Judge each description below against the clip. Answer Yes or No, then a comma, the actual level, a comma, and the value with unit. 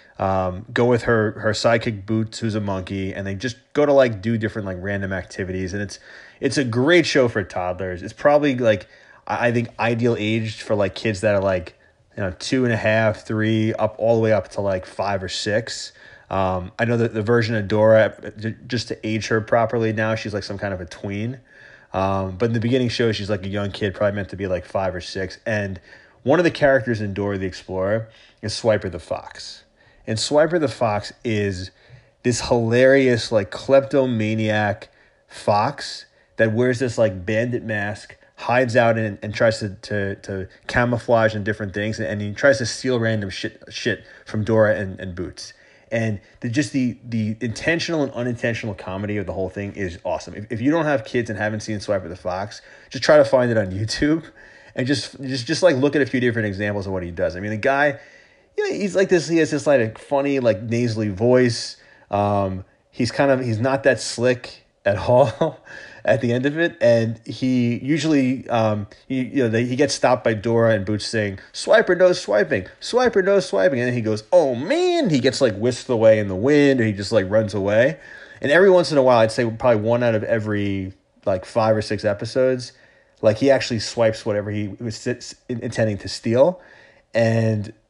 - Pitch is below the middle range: Yes, low, 110 Hz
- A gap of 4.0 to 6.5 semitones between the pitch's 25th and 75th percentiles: No, average, 3.3 semitones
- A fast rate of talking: Yes, fast, 210 wpm